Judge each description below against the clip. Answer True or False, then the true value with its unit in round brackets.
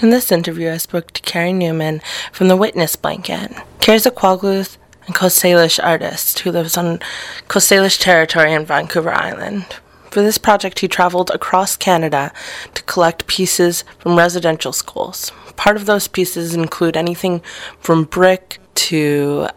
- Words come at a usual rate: True (155 wpm)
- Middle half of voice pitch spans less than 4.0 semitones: True (2.4 semitones)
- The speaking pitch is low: False (175 Hz)